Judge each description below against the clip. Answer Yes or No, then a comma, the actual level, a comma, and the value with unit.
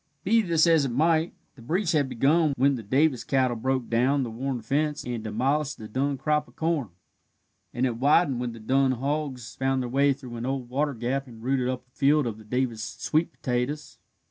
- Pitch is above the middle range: No, low, 135 Hz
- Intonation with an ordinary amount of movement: Yes, average, 3.4 semitones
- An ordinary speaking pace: No, fast, 210 wpm